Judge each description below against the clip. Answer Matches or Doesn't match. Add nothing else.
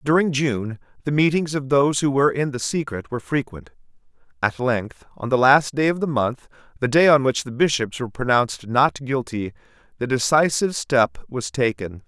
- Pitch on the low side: Matches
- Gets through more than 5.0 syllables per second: Matches